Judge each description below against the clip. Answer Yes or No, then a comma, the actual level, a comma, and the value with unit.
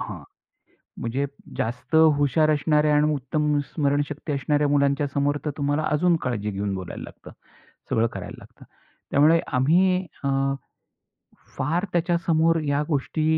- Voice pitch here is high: No, medium, 145 Hz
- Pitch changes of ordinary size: No, narrow, 2.1 semitones